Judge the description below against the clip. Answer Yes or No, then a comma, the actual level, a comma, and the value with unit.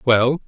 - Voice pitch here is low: Yes, low, 125 Hz